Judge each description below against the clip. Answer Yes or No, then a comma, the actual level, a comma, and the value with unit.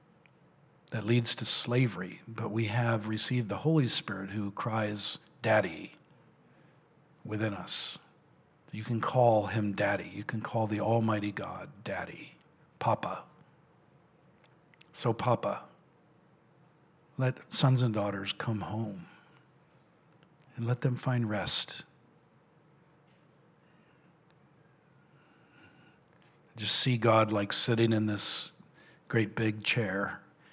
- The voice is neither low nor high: No, low, 120 Hz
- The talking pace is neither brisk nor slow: No, slow, 100 wpm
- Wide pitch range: Yes, wide, 6.2 semitones